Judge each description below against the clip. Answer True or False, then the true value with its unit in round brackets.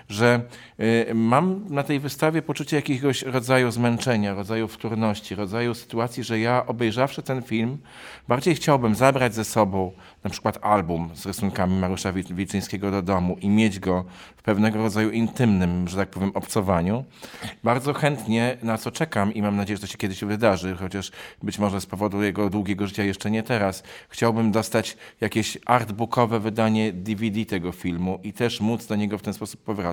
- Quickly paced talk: True (170 wpm)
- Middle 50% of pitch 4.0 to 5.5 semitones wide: False (3.2 semitones)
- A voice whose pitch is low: True (110 Hz)